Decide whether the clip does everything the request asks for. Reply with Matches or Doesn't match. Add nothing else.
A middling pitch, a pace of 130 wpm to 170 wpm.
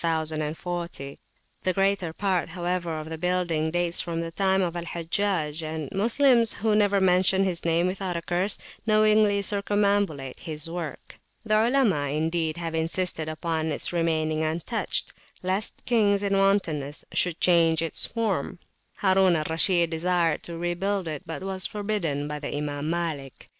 Matches